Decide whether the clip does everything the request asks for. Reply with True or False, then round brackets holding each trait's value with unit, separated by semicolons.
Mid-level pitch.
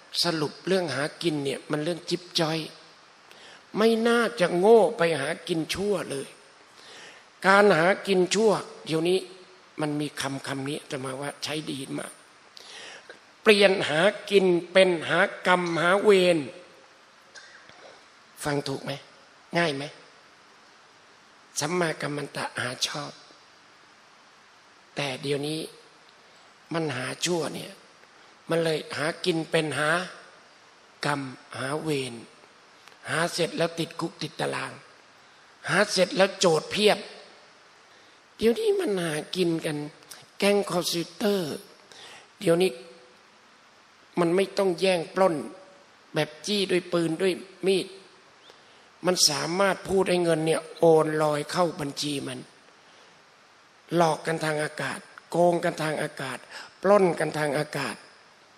True (170 Hz)